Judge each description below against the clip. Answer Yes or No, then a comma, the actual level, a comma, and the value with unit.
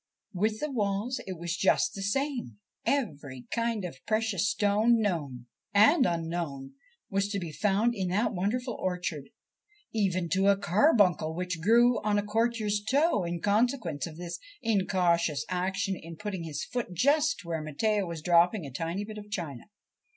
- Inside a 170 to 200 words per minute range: No, average, 160 wpm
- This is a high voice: Yes, high, 195 Hz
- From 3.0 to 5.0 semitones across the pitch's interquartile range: Yes, average, 4.4 semitones